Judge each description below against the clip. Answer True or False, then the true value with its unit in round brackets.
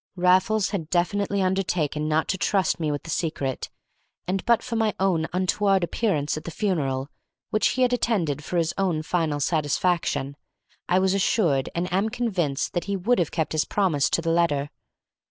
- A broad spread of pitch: False (4.1 semitones)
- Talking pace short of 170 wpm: False (175 wpm)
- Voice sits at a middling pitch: True (175 Hz)